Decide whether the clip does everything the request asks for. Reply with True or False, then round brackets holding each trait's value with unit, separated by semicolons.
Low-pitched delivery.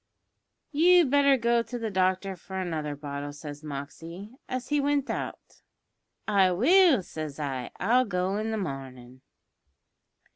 False (190 Hz)